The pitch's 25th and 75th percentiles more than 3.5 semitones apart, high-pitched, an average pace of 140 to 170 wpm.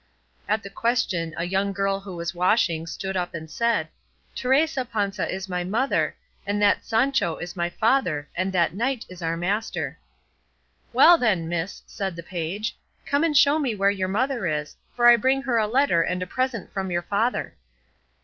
No: average, 5.2 semitones; high, 195 Hz; average, 185 wpm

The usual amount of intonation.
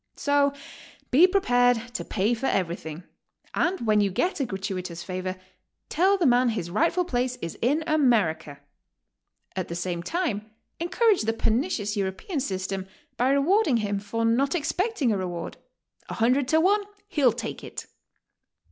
No: wide, 8.0 semitones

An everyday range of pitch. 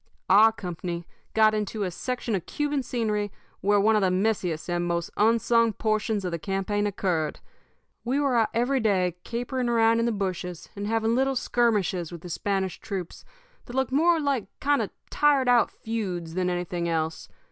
Yes: average, 4.6 semitones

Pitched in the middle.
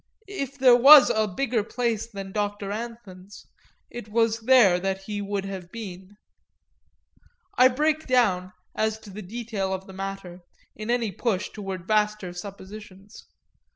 No: high, 210 Hz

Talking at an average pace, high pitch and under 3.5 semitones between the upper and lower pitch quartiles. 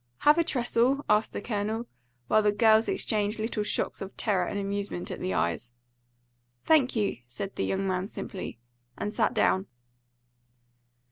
Yes: average, 155 wpm; high, 210 Hz; average, 2.8 semitones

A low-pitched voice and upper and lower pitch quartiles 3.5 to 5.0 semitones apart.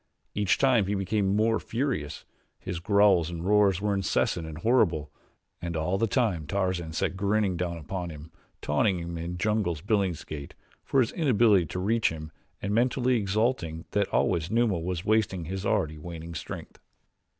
Yes: very low, 95 Hz; average, 4.2 semitones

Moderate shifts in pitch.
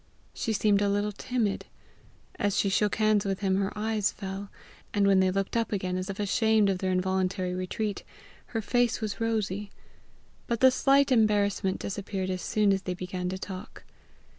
No: narrow, 2.3 semitones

